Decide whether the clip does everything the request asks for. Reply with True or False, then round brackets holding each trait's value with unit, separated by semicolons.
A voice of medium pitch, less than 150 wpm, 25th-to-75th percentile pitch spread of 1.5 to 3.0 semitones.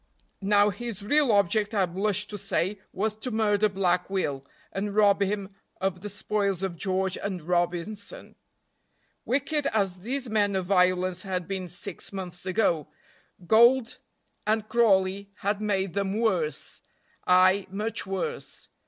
False (200 Hz; 140 wpm; 2.4 semitones)